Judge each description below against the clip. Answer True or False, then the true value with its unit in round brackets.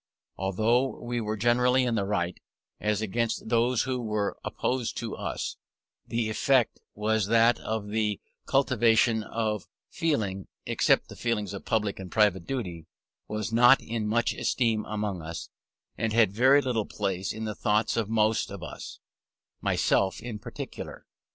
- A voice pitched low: True (110 Hz)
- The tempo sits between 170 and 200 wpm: False (150 wpm)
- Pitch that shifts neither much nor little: False (2.3 semitones)